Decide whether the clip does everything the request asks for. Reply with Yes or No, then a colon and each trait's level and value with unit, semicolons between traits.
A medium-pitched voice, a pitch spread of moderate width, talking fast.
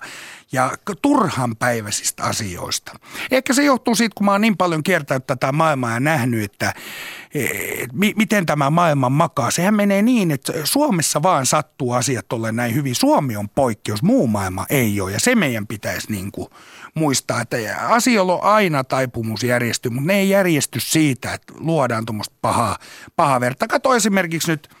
No: medium, 150 Hz; wide, 8.0 semitones; fast, 170 wpm